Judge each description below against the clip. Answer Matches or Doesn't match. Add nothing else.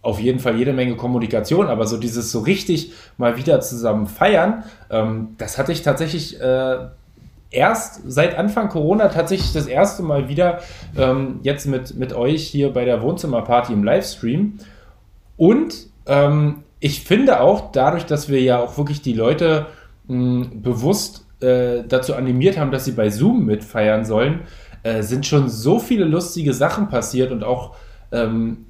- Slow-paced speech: Doesn't match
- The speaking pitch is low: Matches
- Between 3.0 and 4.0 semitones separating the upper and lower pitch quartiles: Doesn't match